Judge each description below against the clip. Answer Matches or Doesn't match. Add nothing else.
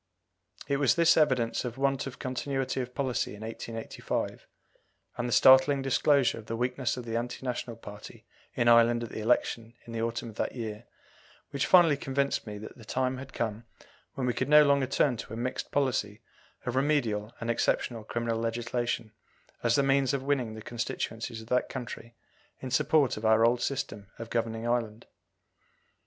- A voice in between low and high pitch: Doesn't match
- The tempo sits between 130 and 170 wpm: Doesn't match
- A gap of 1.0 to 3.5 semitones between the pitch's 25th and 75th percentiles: Matches